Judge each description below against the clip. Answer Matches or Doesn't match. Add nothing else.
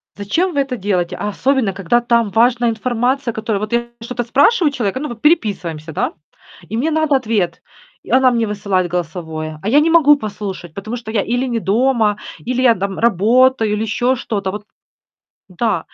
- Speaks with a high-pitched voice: Matches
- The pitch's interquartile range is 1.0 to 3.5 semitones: Doesn't match